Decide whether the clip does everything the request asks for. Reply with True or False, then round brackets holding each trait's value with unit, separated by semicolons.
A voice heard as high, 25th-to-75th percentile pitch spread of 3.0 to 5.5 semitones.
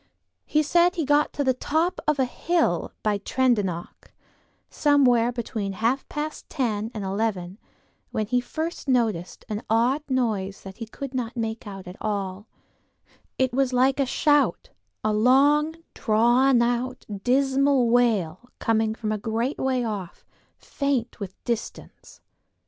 True (240 Hz; 4.2 semitones)